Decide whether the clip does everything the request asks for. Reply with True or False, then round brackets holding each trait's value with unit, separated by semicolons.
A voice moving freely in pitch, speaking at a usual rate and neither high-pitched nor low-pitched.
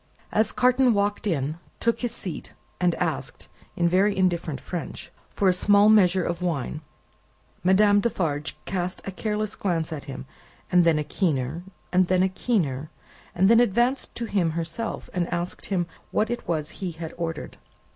False (3.9 semitones; 165 wpm; 180 Hz)